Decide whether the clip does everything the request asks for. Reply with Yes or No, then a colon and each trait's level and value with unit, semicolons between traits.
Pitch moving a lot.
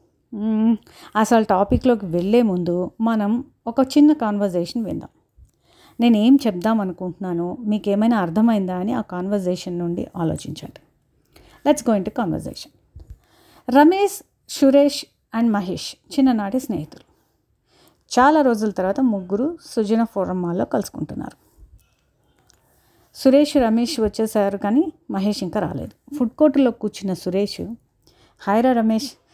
No: average, 4.3 semitones